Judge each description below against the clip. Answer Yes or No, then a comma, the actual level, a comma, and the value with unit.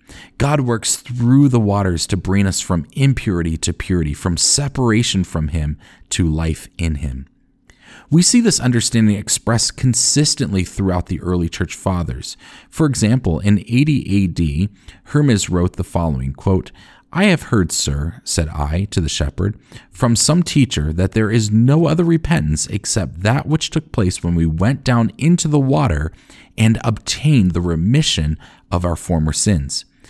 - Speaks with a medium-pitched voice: No, low, 100 Hz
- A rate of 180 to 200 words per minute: No, average, 160 wpm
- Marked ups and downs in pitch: Yes, wide, 6.5 semitones